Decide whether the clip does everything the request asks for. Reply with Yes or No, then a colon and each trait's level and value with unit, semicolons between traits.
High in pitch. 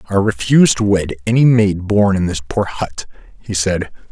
No: low, 100 Hz